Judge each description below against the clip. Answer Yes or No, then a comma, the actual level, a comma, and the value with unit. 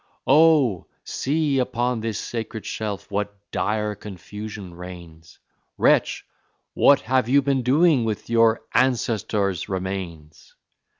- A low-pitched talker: Yes, low, 110 Hz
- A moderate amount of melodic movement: Yes, average, 4.6 semitones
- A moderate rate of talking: No, slow, 110 wpm